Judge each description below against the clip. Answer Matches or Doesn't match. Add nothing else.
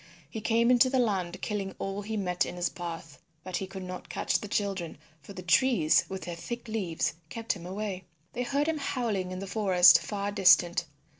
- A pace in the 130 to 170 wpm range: Doesn't match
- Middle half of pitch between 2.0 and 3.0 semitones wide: Doesn't match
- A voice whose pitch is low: Doesn't match